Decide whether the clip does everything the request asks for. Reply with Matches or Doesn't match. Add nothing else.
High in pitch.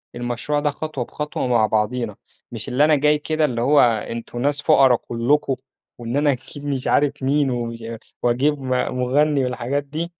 Doesn't match